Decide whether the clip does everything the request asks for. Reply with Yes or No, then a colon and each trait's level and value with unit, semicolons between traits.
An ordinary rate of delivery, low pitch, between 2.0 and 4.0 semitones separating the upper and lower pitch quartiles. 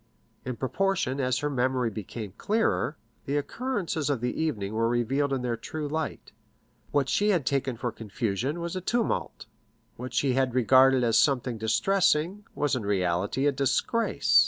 No: average, 160 wpm; low, 130 Hz; average, 4.6 semitones